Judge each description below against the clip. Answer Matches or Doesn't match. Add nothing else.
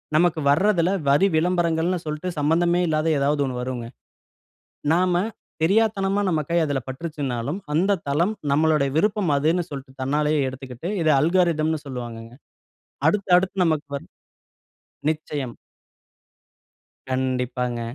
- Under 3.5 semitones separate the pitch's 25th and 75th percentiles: Doesn't match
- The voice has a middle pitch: Matches